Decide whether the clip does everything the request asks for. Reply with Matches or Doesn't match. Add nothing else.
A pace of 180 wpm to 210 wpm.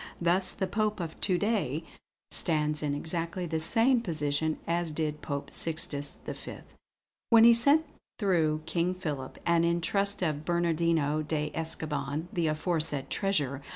Doesn't match